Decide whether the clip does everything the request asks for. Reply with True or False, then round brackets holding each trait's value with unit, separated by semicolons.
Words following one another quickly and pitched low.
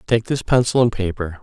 True (210 wpm; 105 Hz)